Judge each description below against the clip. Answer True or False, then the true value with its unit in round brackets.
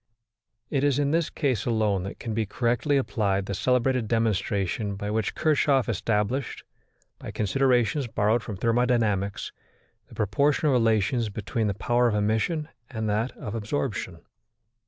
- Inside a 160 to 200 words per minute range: False (140 wpm)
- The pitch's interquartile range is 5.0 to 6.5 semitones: False (3.8 semitones)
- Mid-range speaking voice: False (115 Hz)